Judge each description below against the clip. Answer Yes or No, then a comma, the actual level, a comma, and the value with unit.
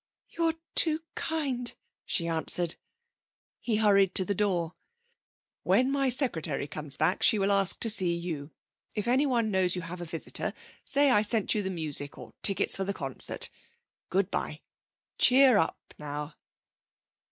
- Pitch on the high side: Yes, high, 195 Hz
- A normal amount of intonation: No, wide, 6.1 semitones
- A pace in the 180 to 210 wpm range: No, average, 155 wpm